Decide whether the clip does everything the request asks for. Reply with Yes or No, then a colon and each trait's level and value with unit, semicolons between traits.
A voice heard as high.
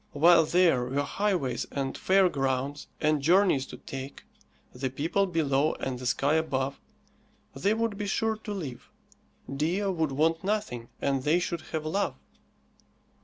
No: medium, 155 Hz